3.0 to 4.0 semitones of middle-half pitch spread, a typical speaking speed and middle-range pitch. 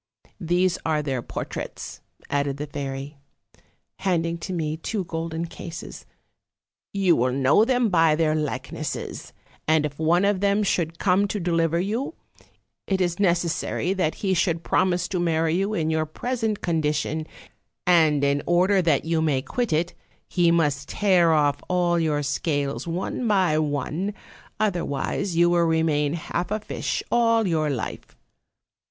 Yes: average, 3.4 semitones; average, 150 wpm; medium, 165 Hz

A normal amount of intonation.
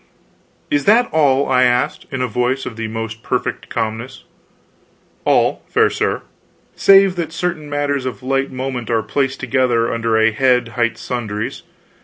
Yes: average, 3.3 semitones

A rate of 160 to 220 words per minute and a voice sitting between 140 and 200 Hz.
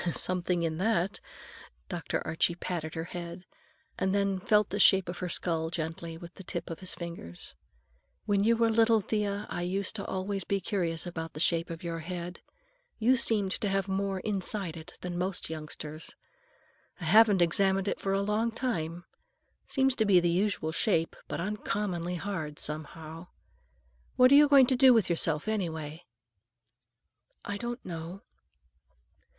Yes: average, 165 wpm; medium, 185 Hz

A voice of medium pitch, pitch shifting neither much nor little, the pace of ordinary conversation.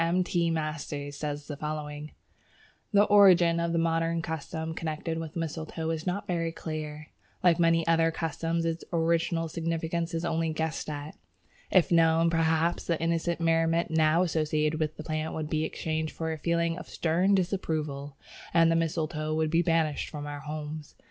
No: medium, 165 Hz; narrow, 1.4 semitones; average, 170 wpm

